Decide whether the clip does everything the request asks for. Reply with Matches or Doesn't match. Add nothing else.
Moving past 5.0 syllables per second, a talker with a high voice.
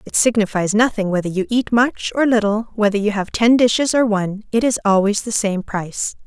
Matches